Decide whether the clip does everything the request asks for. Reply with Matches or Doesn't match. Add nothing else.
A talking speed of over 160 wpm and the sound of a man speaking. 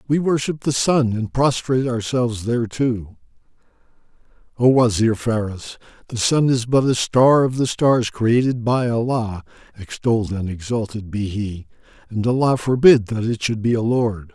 Doesn't match